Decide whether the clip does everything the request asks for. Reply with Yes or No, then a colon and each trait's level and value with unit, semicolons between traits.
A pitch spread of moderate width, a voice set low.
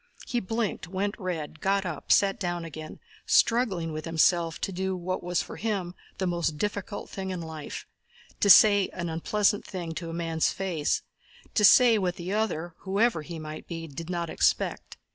No: average, 3.2 semitones; medium, 180 Hz